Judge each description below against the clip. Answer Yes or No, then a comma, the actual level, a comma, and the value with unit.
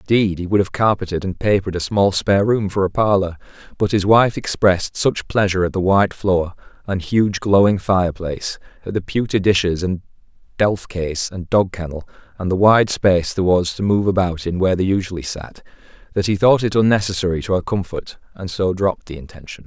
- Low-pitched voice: Yes, very low, 95 Hz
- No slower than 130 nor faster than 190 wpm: No, average, 200 wpm